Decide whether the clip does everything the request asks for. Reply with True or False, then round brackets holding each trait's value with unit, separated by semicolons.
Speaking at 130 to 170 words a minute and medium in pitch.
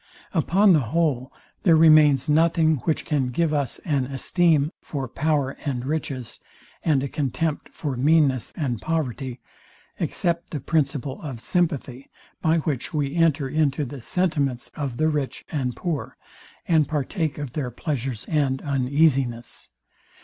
True (140 wpm; 145 Hz)